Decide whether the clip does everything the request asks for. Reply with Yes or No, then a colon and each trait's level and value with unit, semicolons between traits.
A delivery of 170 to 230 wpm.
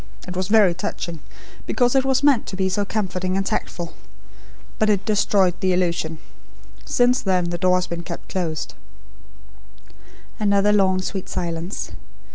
No: average, 150 wpm